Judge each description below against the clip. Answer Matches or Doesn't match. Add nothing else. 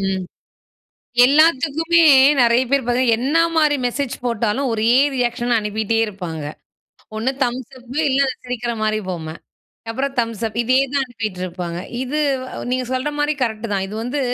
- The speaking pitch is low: Doesn't match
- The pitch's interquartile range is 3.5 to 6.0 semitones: Matches